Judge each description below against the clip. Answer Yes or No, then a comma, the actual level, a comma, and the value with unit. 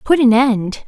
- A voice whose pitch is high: Yes, high, 245 Hz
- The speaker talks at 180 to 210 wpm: Yes, fast, 205 wpm